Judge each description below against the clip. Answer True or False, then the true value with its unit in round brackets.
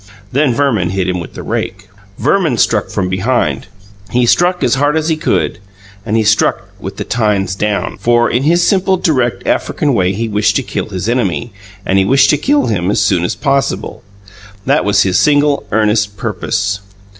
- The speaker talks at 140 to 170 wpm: False (190 wpm)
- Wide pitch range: True (6.0 semitones)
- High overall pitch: False (110 Hz)